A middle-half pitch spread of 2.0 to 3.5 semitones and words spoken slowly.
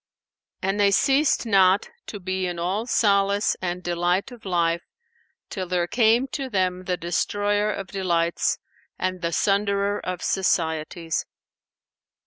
Yes: narrow, 2.6 semitones; slow, 130 wpm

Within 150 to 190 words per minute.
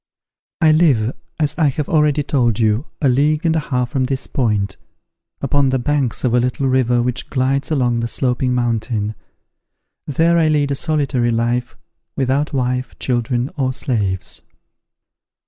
Yes: average, 155 wpm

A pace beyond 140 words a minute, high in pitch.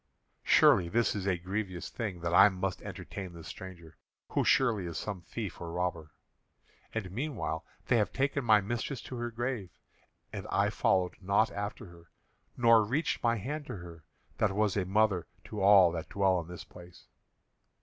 No: average, 180 wpm; low, 100 Hz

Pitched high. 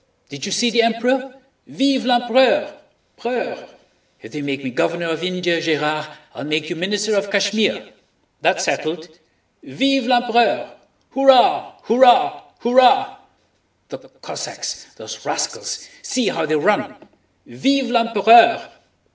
Yes: high, 225 Hz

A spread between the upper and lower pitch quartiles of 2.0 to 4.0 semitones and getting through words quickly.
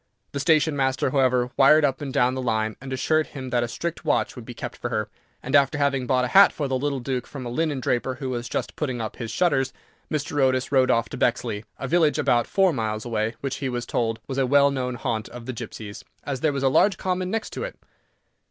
Yes: average, 2.9 semitones; fast, 245 wpm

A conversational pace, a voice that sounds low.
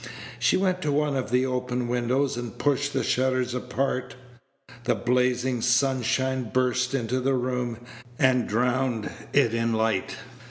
Yes: average, 145 wpm; low, 125 Hz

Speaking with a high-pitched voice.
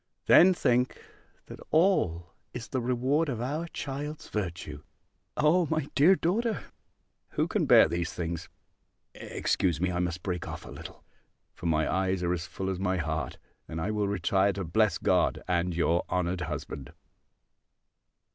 No: very low, 95 Hz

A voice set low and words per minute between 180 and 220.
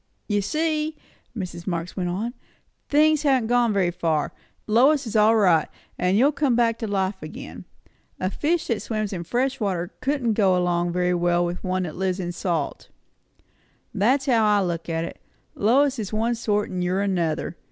No: high, 205 Hz; average, 185 wpm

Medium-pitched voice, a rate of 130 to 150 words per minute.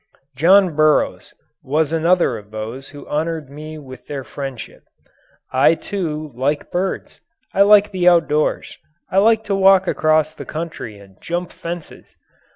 Yes: medium, 155 Hz; average, 140 wpm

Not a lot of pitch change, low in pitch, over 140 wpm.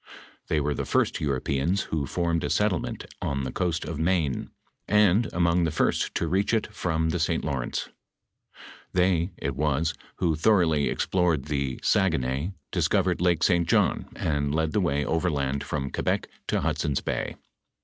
No: average, 3.7 semitones; very low, 80 Hz; average, 165 wpm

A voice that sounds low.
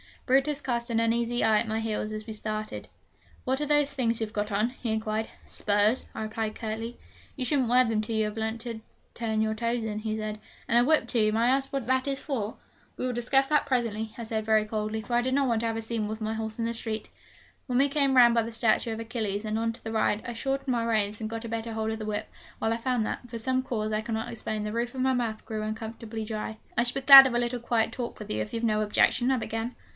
No: high, 225 Hz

